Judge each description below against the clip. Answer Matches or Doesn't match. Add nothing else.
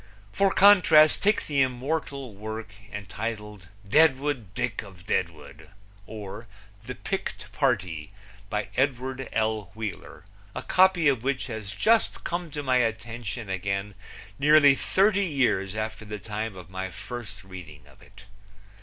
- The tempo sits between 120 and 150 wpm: Matches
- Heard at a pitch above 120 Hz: Doesn't match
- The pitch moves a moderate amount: Doesn't match